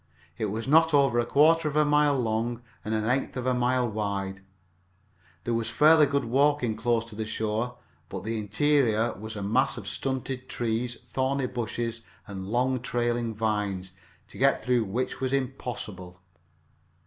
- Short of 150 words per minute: No, average, 165 wpm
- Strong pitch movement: No, average, 3.3 semitones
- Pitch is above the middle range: No, low, 120 Hz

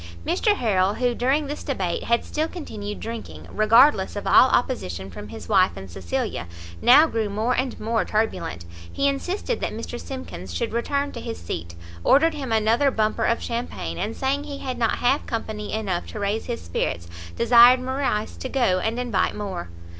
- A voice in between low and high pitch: No, high, 230 Hz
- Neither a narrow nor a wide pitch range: Yes, average, 4.7 semitones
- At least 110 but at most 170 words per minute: No, average, 180 wpm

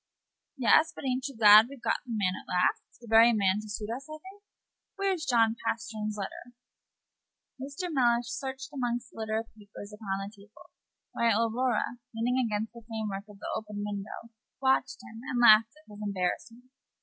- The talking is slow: No, average, 185 wpm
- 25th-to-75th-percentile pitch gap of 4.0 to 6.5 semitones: No, average, 3.3 semitones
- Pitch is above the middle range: Yes, high, 230 Hz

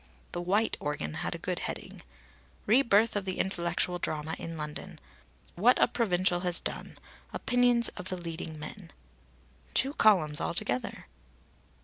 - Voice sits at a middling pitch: Yes, medium, 180 Hz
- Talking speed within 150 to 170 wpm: No, average, 140 wpm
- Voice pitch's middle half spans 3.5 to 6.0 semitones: Yes, average, 4.6 semitones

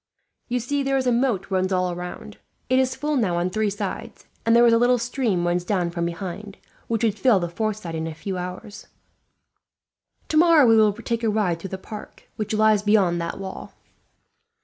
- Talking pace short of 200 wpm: No, fast, 205 wpm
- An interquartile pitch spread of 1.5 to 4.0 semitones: No, average, 4.5 semitones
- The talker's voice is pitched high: Yes, high, 210 Hz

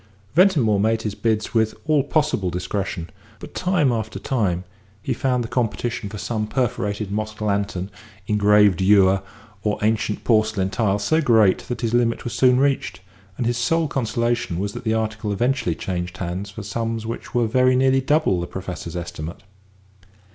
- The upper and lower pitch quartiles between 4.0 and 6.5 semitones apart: No, average, 3.5 semitones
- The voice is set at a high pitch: No, low, 110 Hz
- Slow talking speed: No, average, 165 wpm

